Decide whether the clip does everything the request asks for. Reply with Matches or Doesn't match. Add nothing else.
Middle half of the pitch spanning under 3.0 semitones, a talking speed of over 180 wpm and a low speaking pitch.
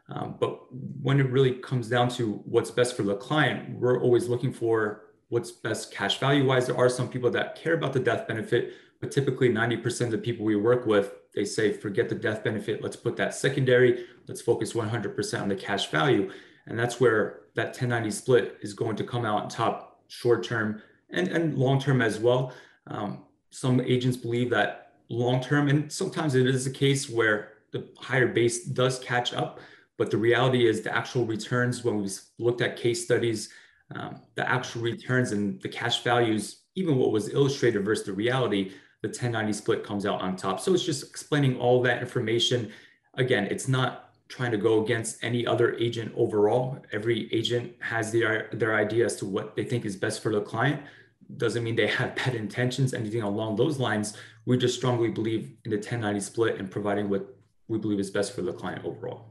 Matches